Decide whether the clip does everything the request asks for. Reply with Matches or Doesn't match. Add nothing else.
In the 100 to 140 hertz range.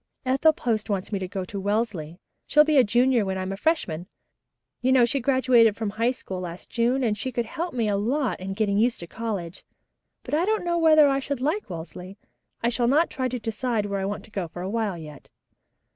Doesn't match